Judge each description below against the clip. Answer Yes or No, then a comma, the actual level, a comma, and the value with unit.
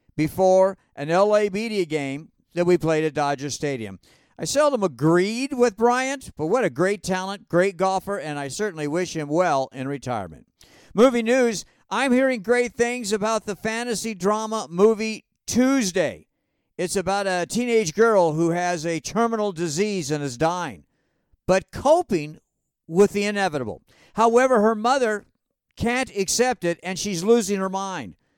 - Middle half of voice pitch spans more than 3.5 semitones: Yes, average, 5.0 semitones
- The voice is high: Yes, high, 195 Hz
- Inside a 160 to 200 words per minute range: No, average, 150 wpm